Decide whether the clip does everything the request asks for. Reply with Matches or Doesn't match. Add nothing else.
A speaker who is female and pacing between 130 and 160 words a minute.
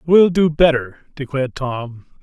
Doesn't match